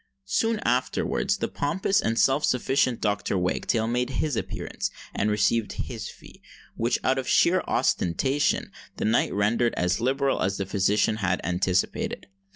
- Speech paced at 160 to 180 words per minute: No, average, 150 wpm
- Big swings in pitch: No, average, 4.8 semitones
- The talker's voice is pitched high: No, low, 115 Hz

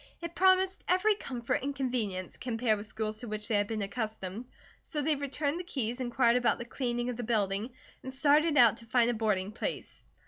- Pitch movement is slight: No, average, 4.6 semitones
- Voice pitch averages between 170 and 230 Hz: No, high, 240 Hz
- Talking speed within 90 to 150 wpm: No, fast, 205 wpm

